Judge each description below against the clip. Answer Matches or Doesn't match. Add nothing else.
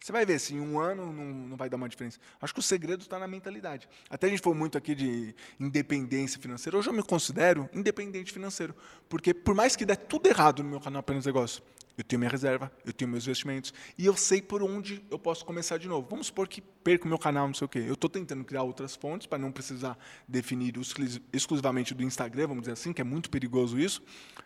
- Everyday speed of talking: Doesn't match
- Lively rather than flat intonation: Matches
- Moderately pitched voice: Matches